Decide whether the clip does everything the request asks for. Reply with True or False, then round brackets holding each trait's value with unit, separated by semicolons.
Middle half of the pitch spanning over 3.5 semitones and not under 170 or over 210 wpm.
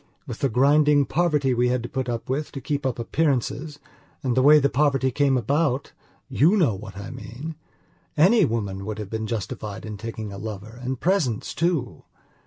True (4.6 semitones; 180 wpm)